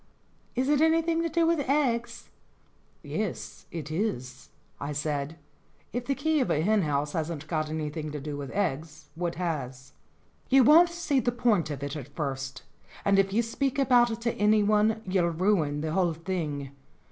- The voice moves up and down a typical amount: No, wide, 8.2 semitones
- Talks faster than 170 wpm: Yes, average, 180 wpm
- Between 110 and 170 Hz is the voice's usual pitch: No, medium, 180 Hz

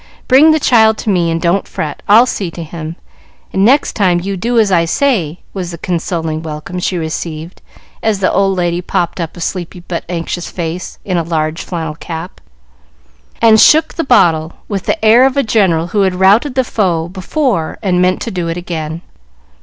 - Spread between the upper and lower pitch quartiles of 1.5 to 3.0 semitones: No, average, 4.2 semitones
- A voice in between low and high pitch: Yes, medium, 180 Hz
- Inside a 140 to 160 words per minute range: No, average, 195 wpm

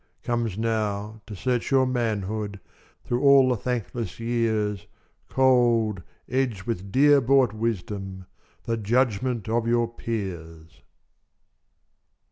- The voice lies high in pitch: No, low, 115 Hz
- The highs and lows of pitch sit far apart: No, average, 3.2 semitones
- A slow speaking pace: Yes, slow, 105 wpm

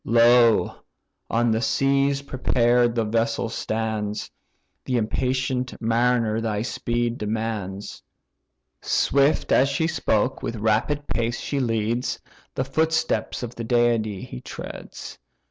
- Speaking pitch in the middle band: No, low, 120 Hz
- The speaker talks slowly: Yes, slow, 115 wpm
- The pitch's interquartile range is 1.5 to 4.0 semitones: Yes, narrow, 2.4 semitones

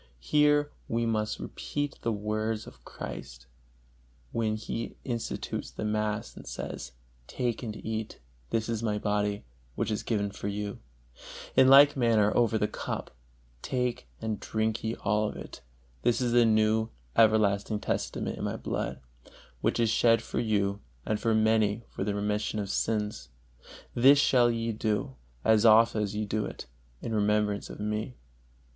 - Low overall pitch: Yes, low, 110 Hz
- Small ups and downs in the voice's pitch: Yes, narrow, 1.7 semitones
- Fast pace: No, average, 160 wpm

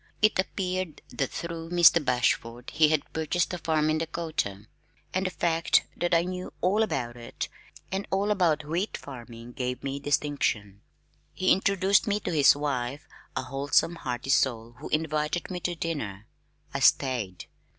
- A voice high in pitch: No, medium, 155 Hz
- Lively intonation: Yes, wide, 5.7 semitones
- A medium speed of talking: Yes, average, 160 wpm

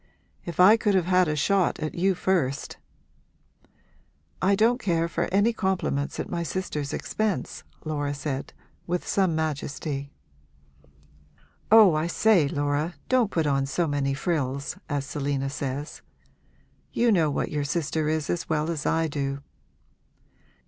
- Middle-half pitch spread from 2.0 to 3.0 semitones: No, average, 4.3 semitones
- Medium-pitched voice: Yes, medium, 160 Hz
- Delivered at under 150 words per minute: Yes, average, 140 wpm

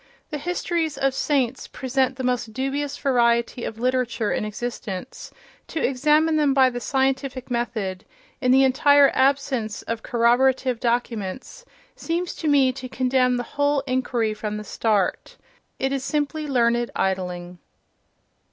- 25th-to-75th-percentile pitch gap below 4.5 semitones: Yes, average, 2.8 semitones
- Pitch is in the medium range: No, very high, 255 Hz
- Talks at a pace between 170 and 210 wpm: No, average, 140 wpm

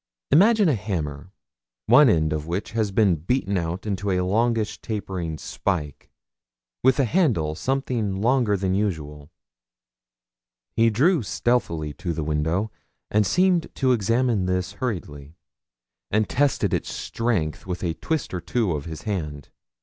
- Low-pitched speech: Yes, low, 100 Hz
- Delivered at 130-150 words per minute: Yes, average, 140 wpm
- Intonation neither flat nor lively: No, wide, 6.4 semitones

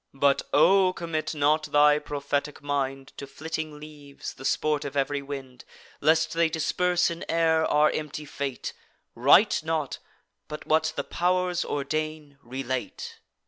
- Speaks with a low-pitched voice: No, medium, 150 Hz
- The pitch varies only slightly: Yes, narrow, 2.2 semitones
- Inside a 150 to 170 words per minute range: No, average, 140 wpm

